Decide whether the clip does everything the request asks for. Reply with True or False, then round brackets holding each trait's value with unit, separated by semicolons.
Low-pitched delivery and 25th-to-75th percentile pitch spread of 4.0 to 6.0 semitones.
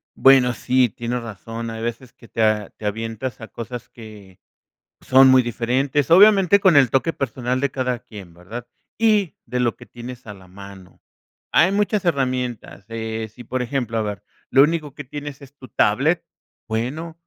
False (125 Hz; 3.6 semitones)